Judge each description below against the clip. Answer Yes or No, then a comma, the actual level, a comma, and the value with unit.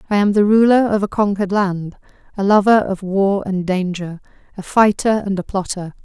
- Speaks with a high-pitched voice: Yes, high, 195 Hz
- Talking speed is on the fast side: No, average, 190 wpm